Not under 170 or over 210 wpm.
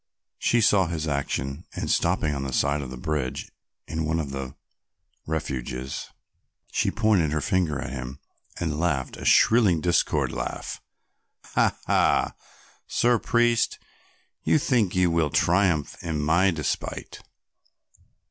No: slow, 135 wpm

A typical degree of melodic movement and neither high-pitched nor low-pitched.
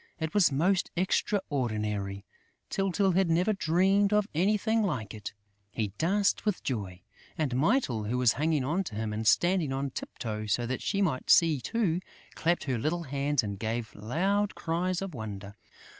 No: wide, 9.0 semitones; medium, 155 Hz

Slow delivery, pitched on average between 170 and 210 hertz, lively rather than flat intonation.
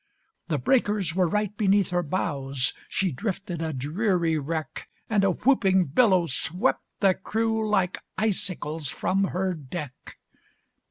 No: slow, 130 wpm; medium, 185 Hz; average, 4.2 semitones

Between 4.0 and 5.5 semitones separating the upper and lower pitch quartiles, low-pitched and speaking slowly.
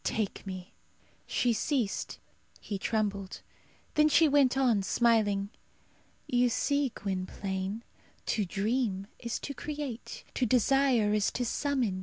No: average, 4.8 semitones; high, 230 Hz; slow, 120 wpm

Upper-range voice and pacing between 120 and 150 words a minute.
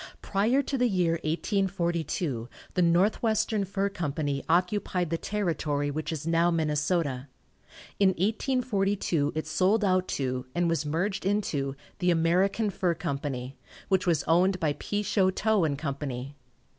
No: medium, 175 Hz; slow, 135 wpm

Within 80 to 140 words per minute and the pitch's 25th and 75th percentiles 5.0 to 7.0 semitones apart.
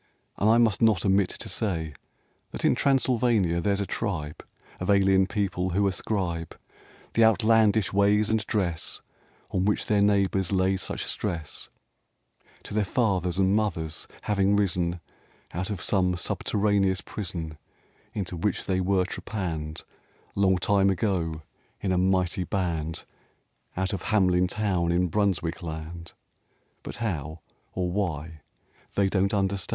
No: slow, 135 wpm; average, 2.7 semitones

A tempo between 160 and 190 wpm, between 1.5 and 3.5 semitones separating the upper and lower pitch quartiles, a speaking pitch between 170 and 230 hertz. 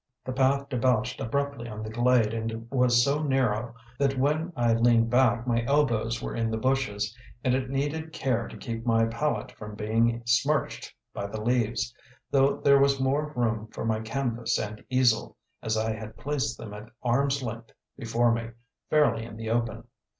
No: average, 180 wpm; average, 2.9 semitones; low, 120 Hz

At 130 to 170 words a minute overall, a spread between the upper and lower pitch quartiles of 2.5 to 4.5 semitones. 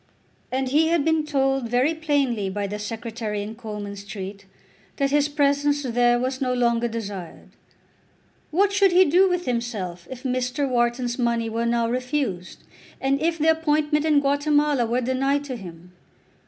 Yes: average, 160 wpm; average, 4.2 semitones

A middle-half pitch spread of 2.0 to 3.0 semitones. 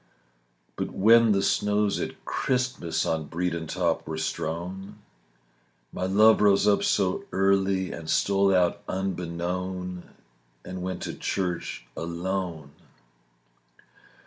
Yes: narrow, 2.4 semitones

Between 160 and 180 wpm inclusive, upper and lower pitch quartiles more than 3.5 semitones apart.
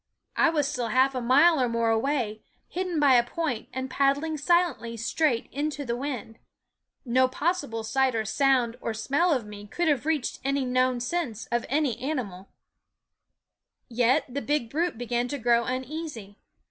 Yes: average, 165 wpm; average, 4.0 semitones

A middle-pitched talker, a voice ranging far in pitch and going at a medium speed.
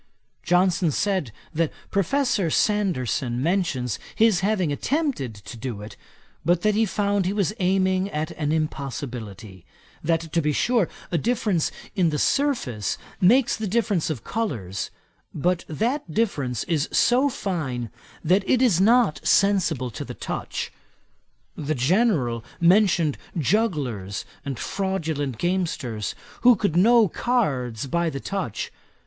No: medium, 170 Hz; wide, 7.1 semitones; slow, 130 wpm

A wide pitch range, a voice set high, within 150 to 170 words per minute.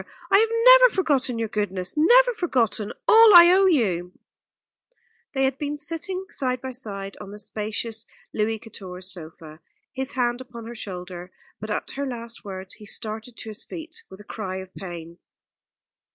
Yes: wide, 6.6 semitones; high, 230 Hz; average, 165 wpm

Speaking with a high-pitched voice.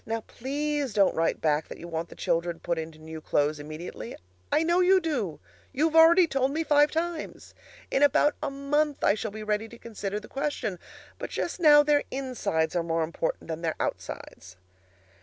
Yes: high, 225 Hz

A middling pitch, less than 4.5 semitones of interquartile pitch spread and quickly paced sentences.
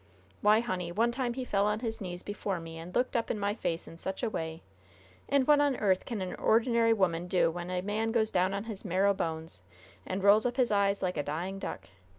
No: high, 200 Hz; average, 4.1 semitones; fast, 235 wpm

